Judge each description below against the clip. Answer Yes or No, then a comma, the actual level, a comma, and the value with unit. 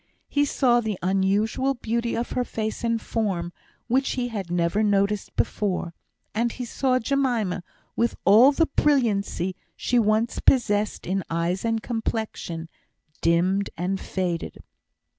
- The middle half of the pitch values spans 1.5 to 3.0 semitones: No, average, 4.0 semitones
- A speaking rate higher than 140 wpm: No, slow, 135 wpm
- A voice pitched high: Yes, high, 215 Hz